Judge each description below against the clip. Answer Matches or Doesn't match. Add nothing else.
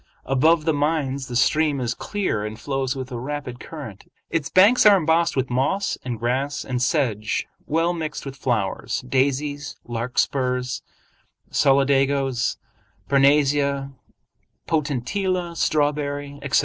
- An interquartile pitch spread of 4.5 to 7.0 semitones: Doesn't match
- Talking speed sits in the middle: Doesn't match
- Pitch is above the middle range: Doesn't match